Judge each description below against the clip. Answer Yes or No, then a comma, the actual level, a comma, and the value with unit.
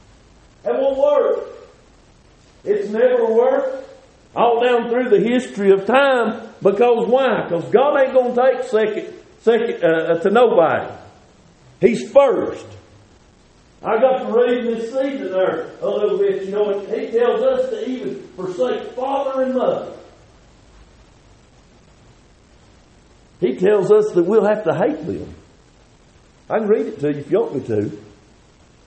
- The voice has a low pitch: No, high, 245 Hz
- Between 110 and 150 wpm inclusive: Yes, average, 145 wpm